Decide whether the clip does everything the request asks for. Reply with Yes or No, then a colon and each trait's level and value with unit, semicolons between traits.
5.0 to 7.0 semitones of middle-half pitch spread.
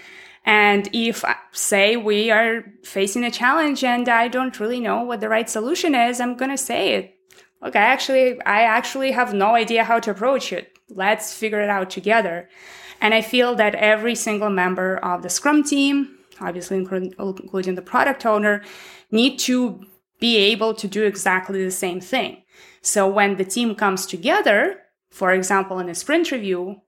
No: average, 4.0 semitones